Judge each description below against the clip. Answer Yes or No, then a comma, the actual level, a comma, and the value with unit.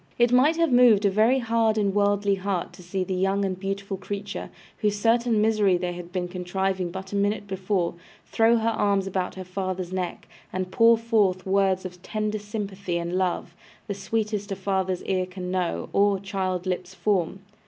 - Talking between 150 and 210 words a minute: Yes, average, 185 wpm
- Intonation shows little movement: Yes, narrow, 2.2 semitones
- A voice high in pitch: Yes, high, 195 Hz